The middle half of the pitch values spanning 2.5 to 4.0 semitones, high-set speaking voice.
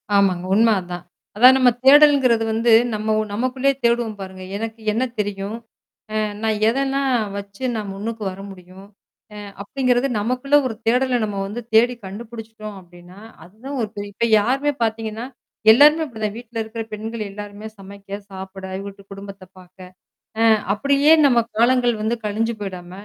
Yes: average, 3.4 semitones; high, 220 Hz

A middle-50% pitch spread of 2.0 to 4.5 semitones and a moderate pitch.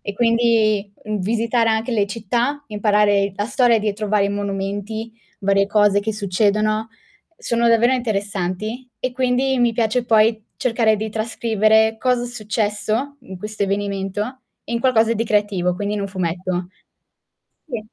No: narrow, 2.5 semitones; high, 215 Hz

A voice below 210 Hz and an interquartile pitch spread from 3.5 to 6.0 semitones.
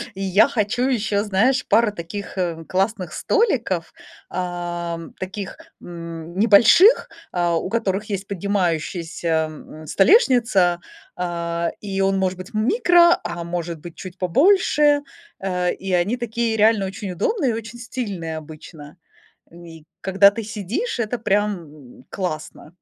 Yes: high, 190 Hz; average, 4.5 semitones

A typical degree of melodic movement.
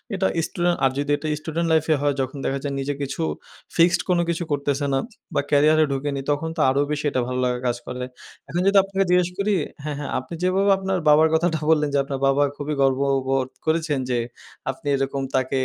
Yes: average, 3.5 semitones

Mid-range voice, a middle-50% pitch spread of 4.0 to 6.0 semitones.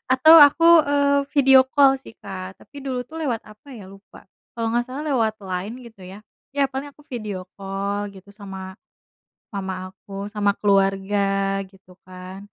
No: high, 205 Hz; average, 5.2 semitones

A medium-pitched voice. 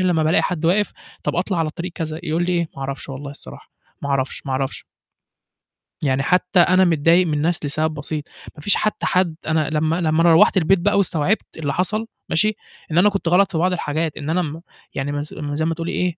Yes: medium, 165 Hz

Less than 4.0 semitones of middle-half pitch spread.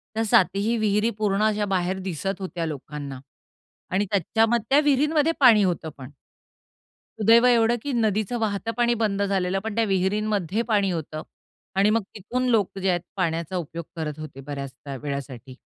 No: average, 5.0 semitones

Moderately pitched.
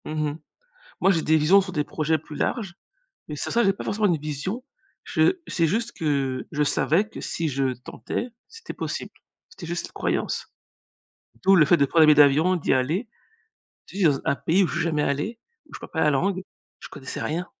Yes: medium, 160 Hz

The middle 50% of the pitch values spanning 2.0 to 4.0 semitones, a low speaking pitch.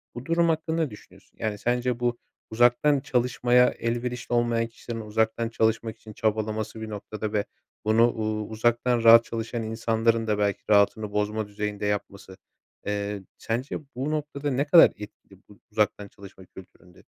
Yes: narrow, 2.5 semitones; low, 110 Hz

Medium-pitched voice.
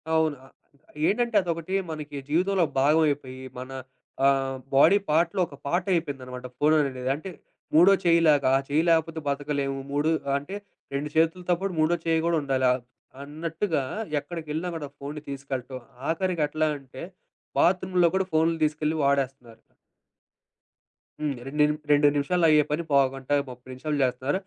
Yes: medium, 150 Hz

